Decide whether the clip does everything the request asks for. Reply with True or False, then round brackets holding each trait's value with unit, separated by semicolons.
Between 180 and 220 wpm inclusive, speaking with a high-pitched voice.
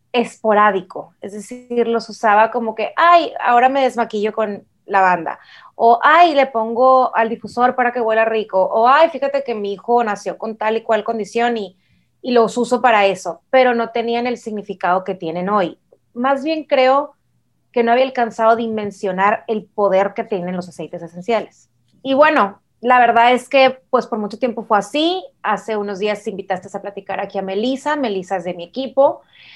True (190 wpm; 225 Hz)